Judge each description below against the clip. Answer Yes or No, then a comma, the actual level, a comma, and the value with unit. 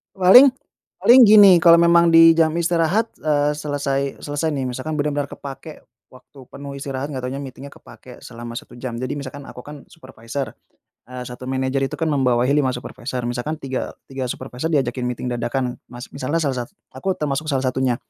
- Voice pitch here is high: No, medium, 140 Hz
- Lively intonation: No, average, 3.5 semitones